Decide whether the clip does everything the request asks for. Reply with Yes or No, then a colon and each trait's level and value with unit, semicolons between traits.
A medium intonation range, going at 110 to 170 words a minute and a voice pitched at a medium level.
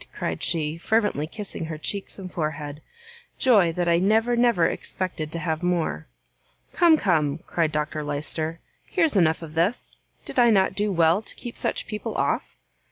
Yes: average, 5.0 semitones; average, 165 wpm; medium, 170 Hz